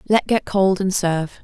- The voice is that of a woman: Yes, female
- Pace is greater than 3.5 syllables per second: Yes, 4.7 syllables/s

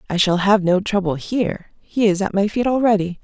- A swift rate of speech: Yes, fast, 220 wpm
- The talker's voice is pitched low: No, high, 200 Hz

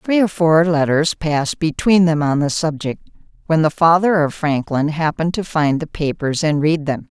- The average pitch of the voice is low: No, medium, 160 Hz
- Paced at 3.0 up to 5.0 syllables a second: Yes, 4.8 syllables/s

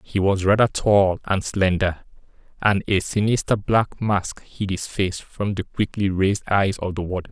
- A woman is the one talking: No, male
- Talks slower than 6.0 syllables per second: Yes, 4.5 syllables/s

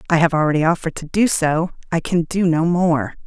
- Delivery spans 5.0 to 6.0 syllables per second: Yes, 5.8 syllables/s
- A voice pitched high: No, medium, 170 Hz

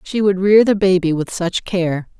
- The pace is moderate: No, fast, 220 wpm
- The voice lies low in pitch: No, medium, 185 Hz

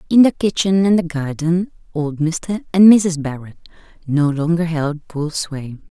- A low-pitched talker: No, medium, 165 Hz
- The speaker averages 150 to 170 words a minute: Yes, average, 160 wpm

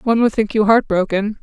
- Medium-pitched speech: No, high, 215 Hz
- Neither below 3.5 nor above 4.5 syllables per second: No, 5.8 syllables/s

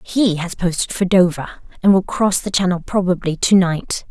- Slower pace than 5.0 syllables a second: Yes, 4.8 syllables/s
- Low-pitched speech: No, medium, 185 Hz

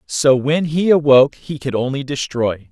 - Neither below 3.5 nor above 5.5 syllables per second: Yes, 4.7 syllables/s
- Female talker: No, male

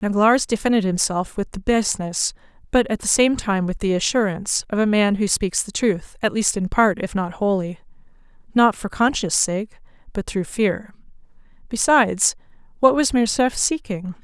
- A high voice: Yes, high, 210 Hz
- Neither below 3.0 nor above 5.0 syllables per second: Yes, 4.9 syllables/s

